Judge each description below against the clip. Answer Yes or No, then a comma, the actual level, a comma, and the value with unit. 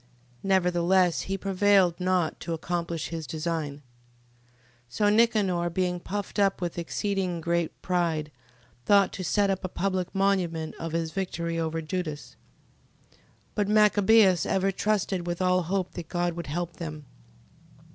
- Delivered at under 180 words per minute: Yes, average, 145 wpm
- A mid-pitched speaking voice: Yes, medium, 180 Hz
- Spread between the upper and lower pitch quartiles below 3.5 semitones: Yes, narrow, 2.6 semitones